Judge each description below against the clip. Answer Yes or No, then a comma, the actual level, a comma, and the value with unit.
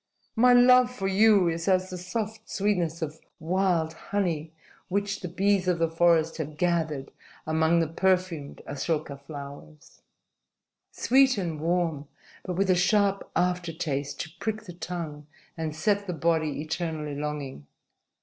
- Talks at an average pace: Yes, average, 145 wpm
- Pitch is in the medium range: Yes, medium, 170 Hz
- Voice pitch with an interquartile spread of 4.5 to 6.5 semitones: No, average, 3.6 semitones